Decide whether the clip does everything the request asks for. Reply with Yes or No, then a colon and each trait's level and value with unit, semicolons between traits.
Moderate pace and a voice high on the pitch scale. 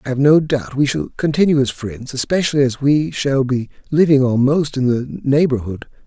No: average, 190 wpm; low, 135 Hz